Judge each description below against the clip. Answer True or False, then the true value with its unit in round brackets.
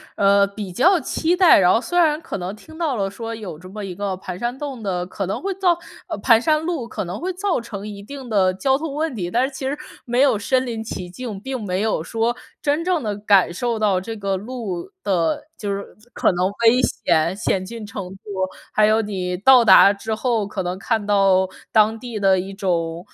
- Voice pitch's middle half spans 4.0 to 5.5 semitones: True (5.1 semitones)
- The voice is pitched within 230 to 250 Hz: False (215 Hz)